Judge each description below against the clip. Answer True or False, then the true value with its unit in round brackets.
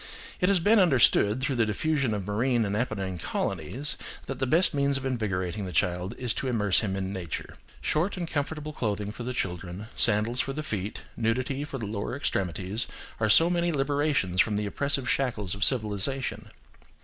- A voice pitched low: True (120 Hz)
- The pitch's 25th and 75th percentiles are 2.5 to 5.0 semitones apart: False (5.5 semitones)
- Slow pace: False (180 wpm)